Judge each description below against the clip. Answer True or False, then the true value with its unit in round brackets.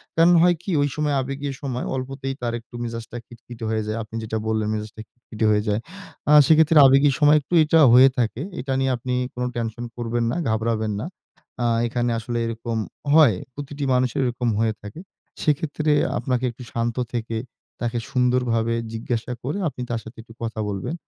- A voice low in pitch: True (120 Hz)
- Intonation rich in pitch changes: False (3.1 semitones)